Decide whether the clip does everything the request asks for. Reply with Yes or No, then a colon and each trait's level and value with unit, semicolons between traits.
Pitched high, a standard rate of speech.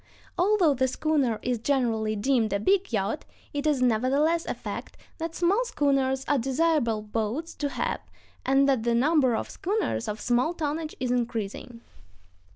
Yes: very high, 265 Hz; average, 160 wpm